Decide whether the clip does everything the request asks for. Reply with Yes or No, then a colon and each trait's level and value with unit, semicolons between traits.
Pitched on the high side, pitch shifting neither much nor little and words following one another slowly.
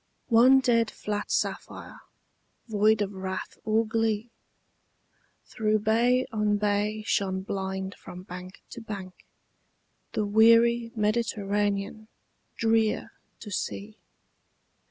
No: high, 215 Hz; narrow, 2.0 semitones; slow, 100 wpm